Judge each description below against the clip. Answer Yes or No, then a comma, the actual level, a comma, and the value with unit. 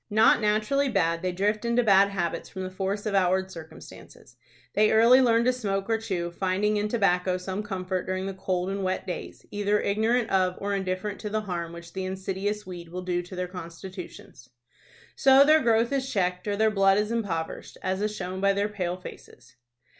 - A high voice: Yes, high, 195 Hz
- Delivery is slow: No, average, 200 wpm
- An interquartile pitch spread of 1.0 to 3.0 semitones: Yes, narrow, 2.5 semitones